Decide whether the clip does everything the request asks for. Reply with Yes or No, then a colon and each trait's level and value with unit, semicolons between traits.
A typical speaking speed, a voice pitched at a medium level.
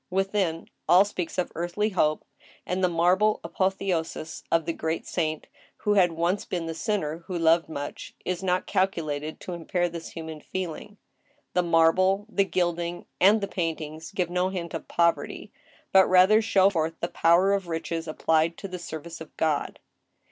Yes: average, 170 wpm; medium, 175 Hz